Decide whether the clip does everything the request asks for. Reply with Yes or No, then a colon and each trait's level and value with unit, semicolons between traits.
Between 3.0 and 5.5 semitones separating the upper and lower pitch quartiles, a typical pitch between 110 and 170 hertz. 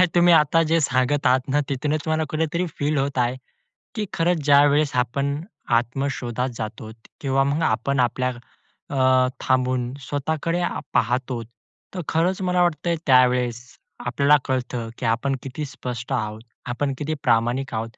Yes: average, 3.4 semitones; low, 135 Hz